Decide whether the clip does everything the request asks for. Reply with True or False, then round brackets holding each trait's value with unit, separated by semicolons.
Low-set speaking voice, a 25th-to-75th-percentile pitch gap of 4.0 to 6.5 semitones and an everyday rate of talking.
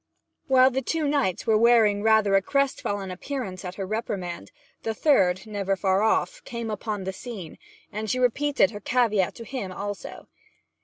False (215 Hz; 4.4 semitones; 170 wpm)